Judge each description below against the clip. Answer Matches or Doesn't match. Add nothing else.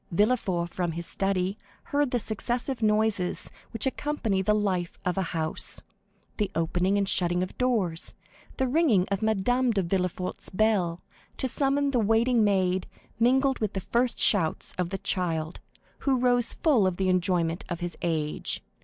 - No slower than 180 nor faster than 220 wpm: Doesn't match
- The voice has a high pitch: Matches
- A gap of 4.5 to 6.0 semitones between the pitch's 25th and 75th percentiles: Matches